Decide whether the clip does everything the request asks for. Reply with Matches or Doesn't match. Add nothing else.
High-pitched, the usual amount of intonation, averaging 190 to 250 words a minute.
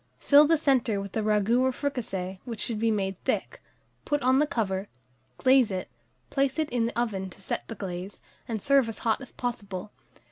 Matches